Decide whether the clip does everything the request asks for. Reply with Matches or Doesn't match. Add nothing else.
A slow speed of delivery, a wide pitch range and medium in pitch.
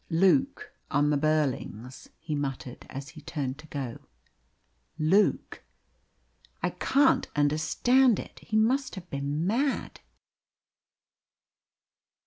Matches